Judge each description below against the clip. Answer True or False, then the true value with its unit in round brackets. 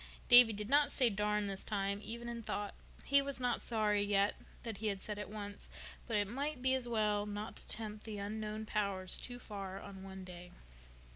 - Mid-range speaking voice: False (210 Hz)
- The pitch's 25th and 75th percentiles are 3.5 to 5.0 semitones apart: False (2.6 semitones)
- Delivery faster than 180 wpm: True (195 wpm)